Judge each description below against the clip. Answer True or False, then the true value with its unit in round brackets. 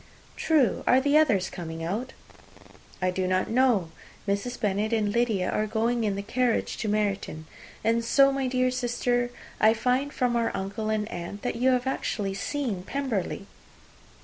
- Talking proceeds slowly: False (165 wpm)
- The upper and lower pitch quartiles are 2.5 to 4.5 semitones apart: True (4.0 semitones)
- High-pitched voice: True (225 Hz)